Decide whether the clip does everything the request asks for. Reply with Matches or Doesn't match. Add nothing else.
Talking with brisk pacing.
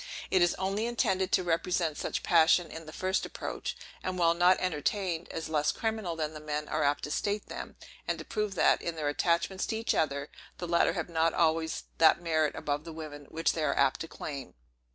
Matches